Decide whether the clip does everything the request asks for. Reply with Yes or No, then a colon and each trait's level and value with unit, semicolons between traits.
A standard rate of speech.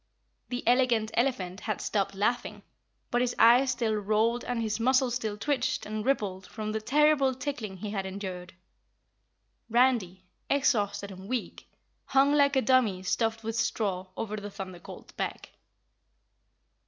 Yes: average, 145 wpm